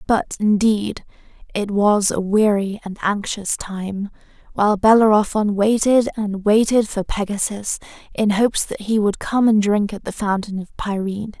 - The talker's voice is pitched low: No, high, 205 Hz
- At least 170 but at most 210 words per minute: No, average, 155 wpm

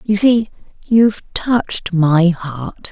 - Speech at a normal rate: No, slow, 125 wpm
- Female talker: Yes, female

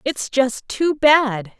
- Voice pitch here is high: Yes, very high, 265 Hz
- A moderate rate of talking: Yes, average, 150 wpm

